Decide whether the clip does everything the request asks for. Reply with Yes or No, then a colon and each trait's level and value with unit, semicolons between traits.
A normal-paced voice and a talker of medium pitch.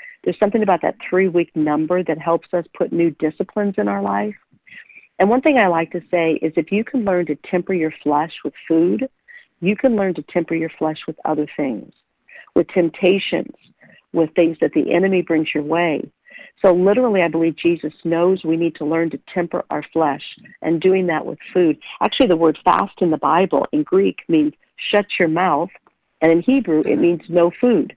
Yes: average, 195 wpm; medium, 170 Hz